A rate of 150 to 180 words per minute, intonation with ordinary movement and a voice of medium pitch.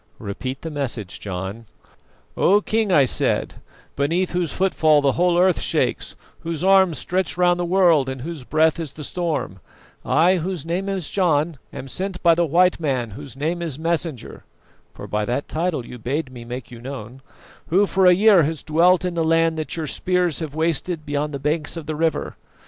No: average, 190 wpm; average, 4.3 semitones; medium, 160 Hz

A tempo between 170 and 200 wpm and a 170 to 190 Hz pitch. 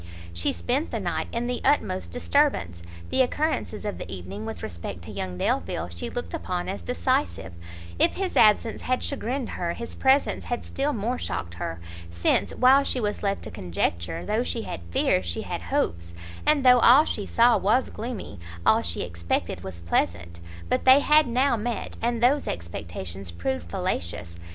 Yes: average, 175 wpm; medium, 185 Hz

